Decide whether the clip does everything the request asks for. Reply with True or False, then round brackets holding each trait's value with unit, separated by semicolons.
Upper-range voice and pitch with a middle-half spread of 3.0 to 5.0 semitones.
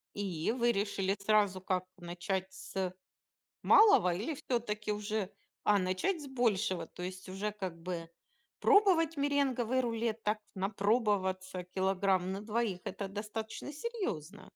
True (205 Hz; 3.9 semitones)